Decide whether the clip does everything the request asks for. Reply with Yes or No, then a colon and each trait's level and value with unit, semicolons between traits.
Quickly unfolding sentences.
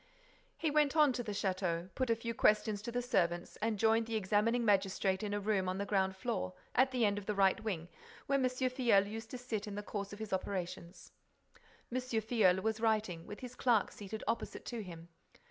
Yes: fast, 215 wpm